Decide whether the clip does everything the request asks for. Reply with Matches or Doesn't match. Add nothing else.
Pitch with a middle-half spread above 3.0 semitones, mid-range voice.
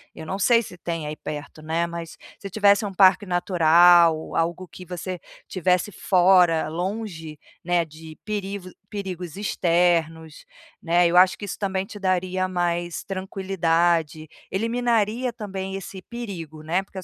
Doesn't match